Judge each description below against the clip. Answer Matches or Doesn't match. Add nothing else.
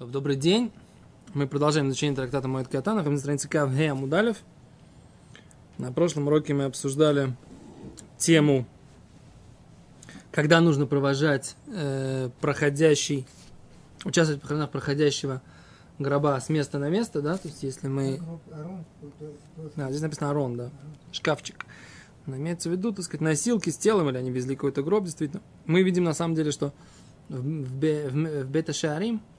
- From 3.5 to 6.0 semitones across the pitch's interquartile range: Doesn't match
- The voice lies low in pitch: Doesn't match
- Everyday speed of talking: Matches